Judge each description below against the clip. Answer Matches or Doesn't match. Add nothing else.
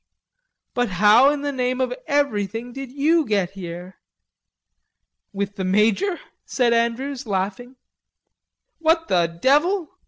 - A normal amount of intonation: Doesn't match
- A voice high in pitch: Matches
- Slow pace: Matches